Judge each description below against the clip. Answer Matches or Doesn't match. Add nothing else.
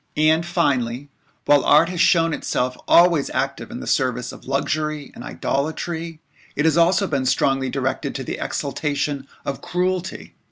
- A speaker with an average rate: Matches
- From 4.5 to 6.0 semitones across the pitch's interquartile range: Doesn't match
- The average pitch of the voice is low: Doesn't match